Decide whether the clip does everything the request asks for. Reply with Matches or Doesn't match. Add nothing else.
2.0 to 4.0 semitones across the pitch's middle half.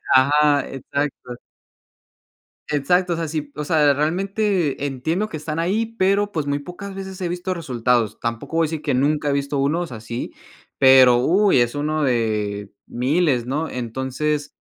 Doesn't match